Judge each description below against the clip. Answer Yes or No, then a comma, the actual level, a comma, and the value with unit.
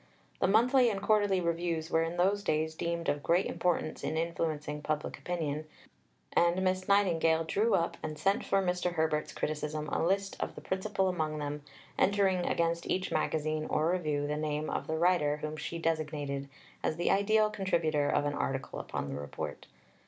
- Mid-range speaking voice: Yes, medium, 165 Hz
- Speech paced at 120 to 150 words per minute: No, average, 175 wpm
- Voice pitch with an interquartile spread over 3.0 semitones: Yes, average, 3.4 semitones